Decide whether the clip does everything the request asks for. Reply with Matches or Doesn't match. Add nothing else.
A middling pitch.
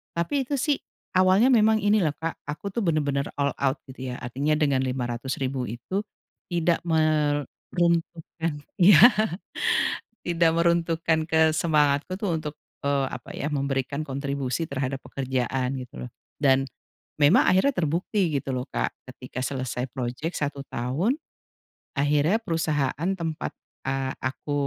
Matches